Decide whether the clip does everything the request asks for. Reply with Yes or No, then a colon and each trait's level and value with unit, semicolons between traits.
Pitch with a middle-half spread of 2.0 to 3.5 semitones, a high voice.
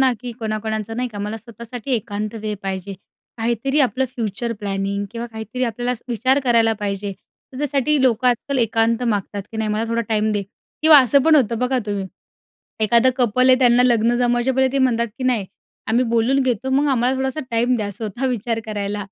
Yes: average, 2.9 semitones; high, 235 Hz